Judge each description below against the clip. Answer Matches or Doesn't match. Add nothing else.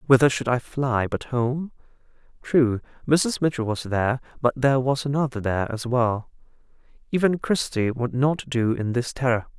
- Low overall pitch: Matches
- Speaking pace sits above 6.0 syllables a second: Doesn't match